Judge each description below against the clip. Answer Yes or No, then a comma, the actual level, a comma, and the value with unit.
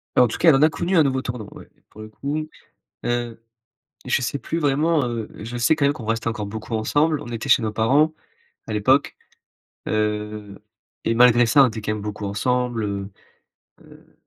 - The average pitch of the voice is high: No, low, 120 Hz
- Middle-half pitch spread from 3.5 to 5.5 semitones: Yes, average, 4.6 semitones